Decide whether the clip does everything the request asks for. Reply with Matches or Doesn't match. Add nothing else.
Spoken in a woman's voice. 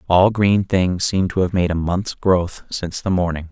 Doesn't match